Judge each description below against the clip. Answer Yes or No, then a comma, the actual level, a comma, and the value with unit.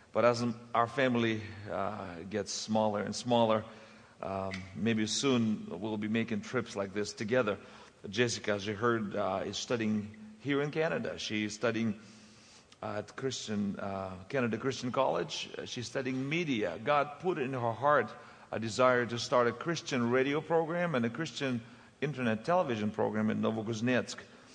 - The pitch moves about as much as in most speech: Yes, average, 3.1 semitones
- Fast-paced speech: No, average, 150 wpm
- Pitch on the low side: Yes, low, 115 Hz